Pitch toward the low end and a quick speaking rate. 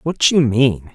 No: low, 130 Hz; average, 190 wpm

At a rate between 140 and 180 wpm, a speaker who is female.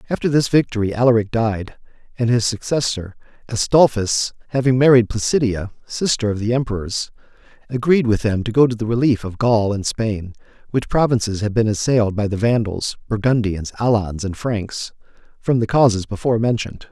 No: average, 160 wpm; male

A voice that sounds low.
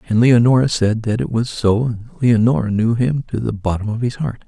Yes: low, 115 Hz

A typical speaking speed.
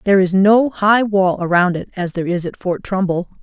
No: fast, 230 wpm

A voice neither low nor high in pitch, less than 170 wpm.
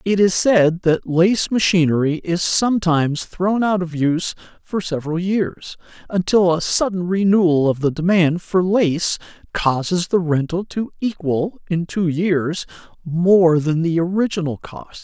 Yes: medium, 175 Hz; average, 150 wpm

